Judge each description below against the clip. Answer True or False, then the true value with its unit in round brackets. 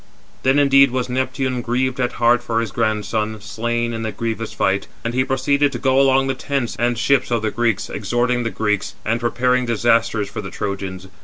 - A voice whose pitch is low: True (120 Hz)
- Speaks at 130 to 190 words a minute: False (200 wpm)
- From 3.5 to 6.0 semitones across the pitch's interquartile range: False (2.8 semitones)